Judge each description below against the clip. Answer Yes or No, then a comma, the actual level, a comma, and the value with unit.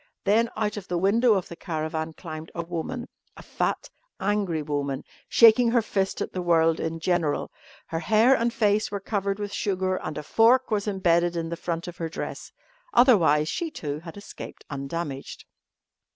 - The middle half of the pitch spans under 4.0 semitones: No, average, 4.5 semitones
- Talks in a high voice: No, medium, 180 Hz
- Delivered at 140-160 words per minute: No, average, 180 wpm